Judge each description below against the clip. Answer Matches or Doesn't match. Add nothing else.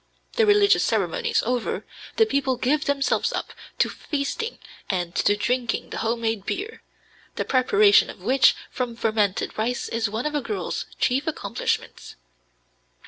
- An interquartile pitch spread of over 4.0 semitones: Matches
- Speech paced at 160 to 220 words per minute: Doesn't match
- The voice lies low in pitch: Doesn't match